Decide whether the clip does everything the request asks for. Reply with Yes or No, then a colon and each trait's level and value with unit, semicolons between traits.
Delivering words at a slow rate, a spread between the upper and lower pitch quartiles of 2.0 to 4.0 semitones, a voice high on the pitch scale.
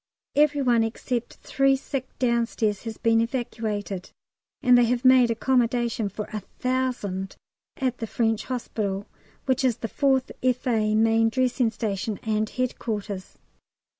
Yes: slow, 130 wpm; average, 2.8 semitones; high, 235 Hz